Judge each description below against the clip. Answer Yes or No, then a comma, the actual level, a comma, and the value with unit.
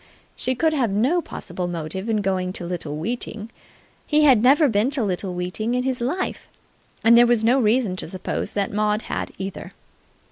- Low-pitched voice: No, high, 220 Hz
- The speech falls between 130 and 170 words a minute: No, average, 185 wpm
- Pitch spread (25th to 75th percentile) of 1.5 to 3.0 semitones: No, average, 5.0 semitones